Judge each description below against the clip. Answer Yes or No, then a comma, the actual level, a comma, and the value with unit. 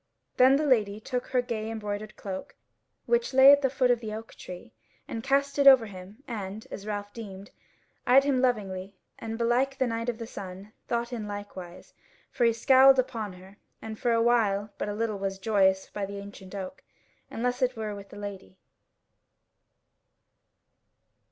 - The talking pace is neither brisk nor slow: Yes, average, 175 wpm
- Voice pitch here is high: Yes, high, 220 Hz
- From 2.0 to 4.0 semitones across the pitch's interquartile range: Yes, average, 3.7 semitones